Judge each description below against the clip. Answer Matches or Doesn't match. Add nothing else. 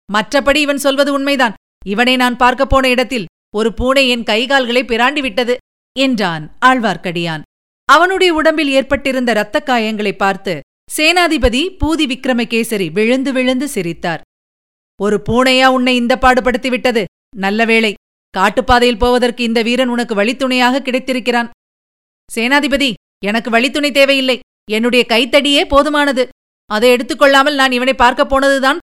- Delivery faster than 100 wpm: Matches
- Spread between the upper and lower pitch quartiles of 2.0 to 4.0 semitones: Matches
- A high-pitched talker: Matches